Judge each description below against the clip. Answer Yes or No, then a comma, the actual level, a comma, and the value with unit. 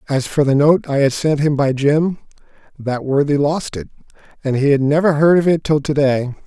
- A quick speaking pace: Yes, fast, 225 wpm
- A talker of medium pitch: Yes, medium, 145 Hz